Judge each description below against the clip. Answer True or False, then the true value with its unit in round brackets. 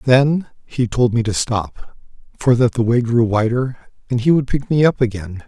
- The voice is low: True (120 Hz)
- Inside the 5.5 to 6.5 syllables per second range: False (4.6 syllables/s)